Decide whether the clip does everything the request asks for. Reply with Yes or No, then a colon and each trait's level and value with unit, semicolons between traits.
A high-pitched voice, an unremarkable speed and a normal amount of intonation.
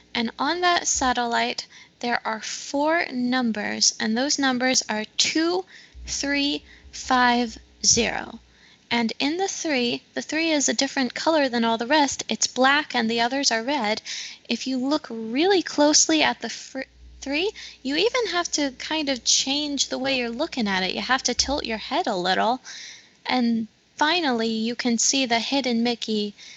Yes: very high, 260 Hz; average, 170 wpm; average, 4.0 semitones